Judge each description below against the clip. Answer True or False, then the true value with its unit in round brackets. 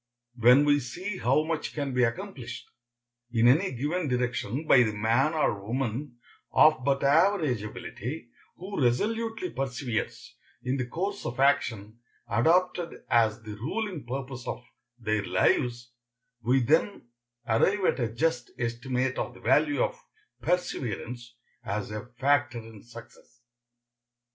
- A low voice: True (125 Hz)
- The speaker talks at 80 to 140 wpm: True (135 wpm)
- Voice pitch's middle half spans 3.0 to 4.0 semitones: False (4.8 semitones)